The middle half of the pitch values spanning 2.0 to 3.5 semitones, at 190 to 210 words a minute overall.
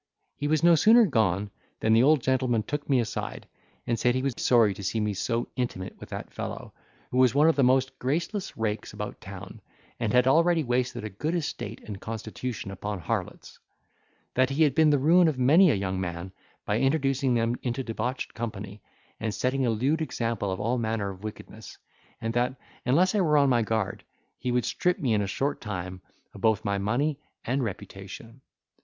No: average, 4.5 semitones; average, 200 wpm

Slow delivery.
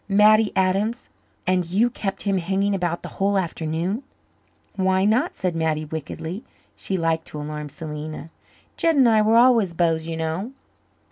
No: average, 155 wpm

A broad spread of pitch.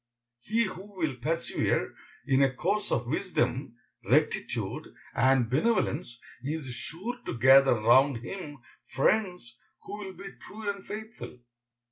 Yes: wide, 7.4 semitones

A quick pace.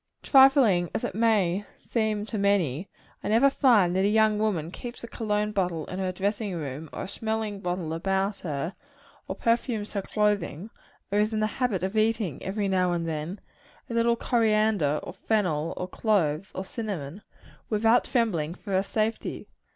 No: average, 175 wpm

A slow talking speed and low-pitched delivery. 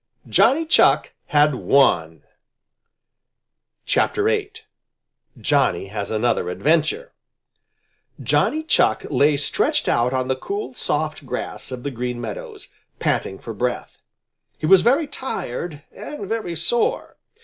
No: slow, 115 wpm; medium, 145 Hz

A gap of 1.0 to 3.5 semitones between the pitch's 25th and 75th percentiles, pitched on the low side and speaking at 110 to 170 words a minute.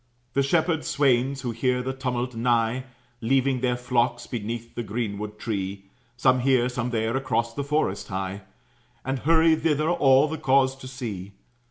Yes: average, 2.8 semitones; low, 125 Hz; average, 160 wpm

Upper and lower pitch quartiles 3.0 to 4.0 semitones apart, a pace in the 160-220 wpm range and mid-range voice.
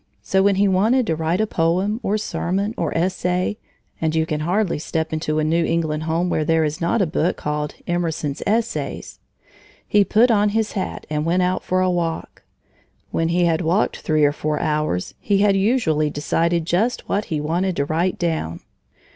Yes: average, 3.7 semitones; average, 190 wpm; medium, 170 Hz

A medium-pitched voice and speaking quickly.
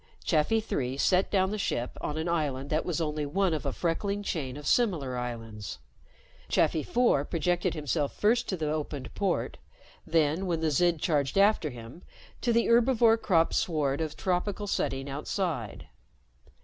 No: medium, 160 Hz; average, 160 wpm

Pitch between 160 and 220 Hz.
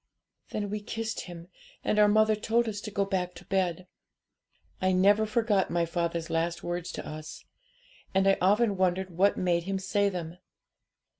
Yes: high, 190 Hz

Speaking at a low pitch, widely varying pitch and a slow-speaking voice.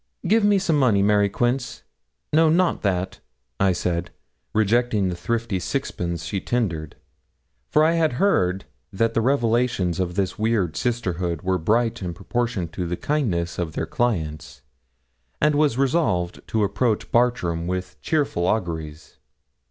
No: low, 105 Hz; wide, 5.8 semitones; average, 145 wpm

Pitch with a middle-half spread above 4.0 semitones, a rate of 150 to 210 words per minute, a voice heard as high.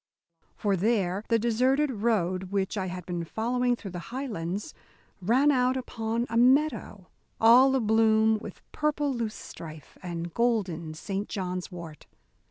No: average, 5.0 semitones; average, 140 wpm; high, 220 Hz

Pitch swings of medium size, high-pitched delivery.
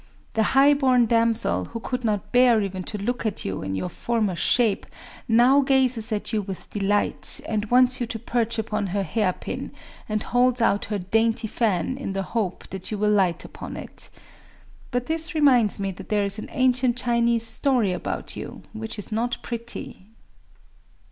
Yes: average, 3.2 semitones; high, 225 Hz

